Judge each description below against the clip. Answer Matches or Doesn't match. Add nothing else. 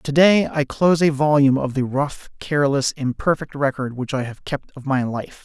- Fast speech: Matches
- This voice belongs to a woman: Doesn't match